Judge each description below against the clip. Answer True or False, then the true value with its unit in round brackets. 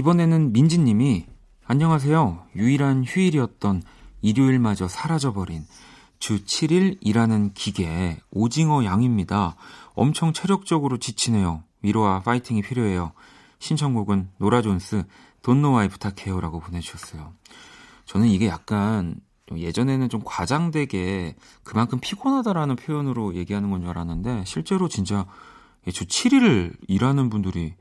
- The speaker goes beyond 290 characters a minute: True (310 characters per minute)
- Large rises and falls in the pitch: True (6.9 semitones)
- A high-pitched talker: False (110 Hz)